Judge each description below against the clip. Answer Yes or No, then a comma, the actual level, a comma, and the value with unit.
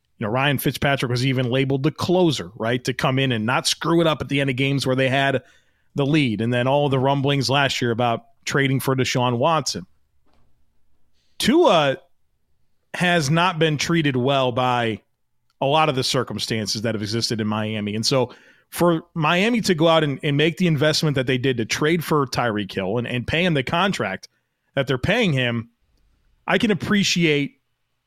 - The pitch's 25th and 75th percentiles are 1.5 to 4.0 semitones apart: No, average, 4.8 semitones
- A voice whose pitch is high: No, low, 135 Hz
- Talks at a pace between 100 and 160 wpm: No, average, 190 wpm